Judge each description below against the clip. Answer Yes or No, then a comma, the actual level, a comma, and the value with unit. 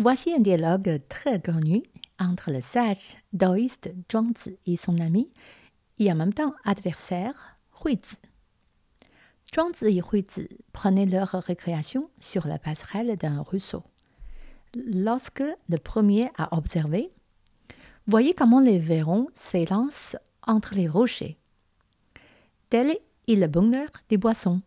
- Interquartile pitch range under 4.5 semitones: No, average, 4.9 semitones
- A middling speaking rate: No, slow, 120 wpm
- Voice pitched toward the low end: No, high, 200 Hz